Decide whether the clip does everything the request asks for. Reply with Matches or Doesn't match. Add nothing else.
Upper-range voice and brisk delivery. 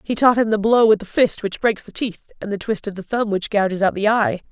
Matches